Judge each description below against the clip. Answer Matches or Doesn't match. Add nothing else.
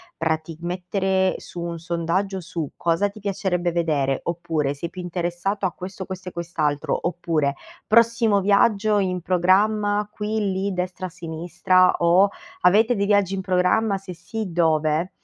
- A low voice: Doesn't match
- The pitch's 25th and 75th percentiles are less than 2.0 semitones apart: Doesn't match